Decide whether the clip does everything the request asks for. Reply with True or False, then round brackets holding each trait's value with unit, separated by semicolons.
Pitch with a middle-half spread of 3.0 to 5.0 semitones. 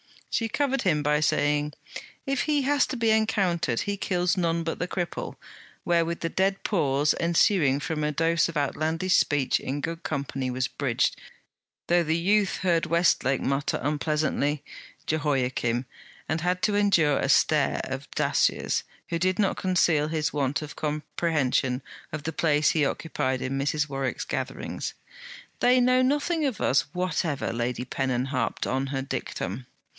True (4.6 semitones)